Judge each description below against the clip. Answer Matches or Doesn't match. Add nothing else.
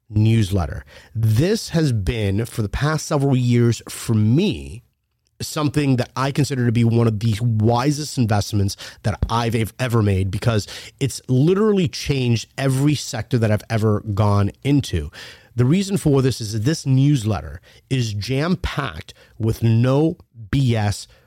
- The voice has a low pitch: Matches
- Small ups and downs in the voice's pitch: Doesn't match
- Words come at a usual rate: Matches